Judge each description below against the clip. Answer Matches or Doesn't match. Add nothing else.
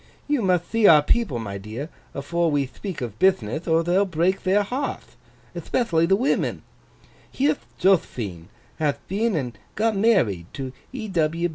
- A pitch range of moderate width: Doesn't match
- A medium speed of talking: Matches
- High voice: Doesn't match